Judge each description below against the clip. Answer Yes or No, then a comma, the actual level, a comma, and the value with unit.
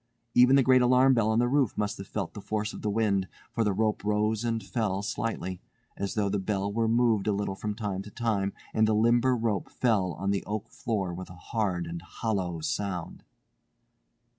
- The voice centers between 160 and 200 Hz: No, low, 105 Hz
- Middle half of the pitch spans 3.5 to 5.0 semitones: No, average, 2.8 semitones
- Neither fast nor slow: No, fast, 210 wpm